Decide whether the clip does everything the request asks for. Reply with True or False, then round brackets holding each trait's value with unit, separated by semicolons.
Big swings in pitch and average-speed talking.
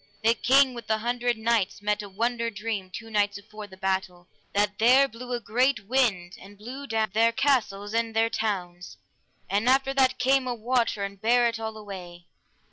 False (3.3 semitones; 190 wpm)